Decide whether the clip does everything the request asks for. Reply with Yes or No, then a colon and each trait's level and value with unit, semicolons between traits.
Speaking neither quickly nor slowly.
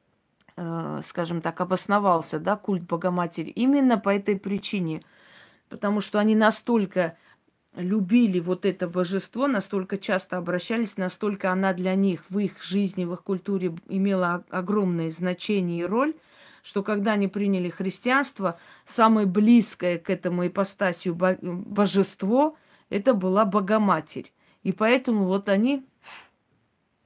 Yes: average, 120 wpm